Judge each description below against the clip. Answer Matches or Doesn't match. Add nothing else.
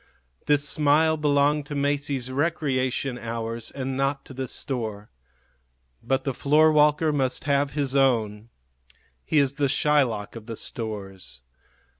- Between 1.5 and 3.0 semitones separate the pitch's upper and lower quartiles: Doesn't match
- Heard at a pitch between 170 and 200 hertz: Doesn't match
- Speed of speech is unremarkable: Doesn't match